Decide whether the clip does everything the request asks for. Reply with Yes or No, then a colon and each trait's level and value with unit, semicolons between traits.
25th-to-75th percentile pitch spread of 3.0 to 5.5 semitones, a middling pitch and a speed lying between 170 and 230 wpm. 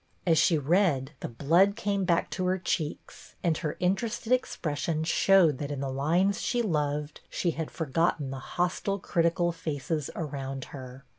No: average, 4.3 semitones; medium, 165 Hz; average, 160 wpm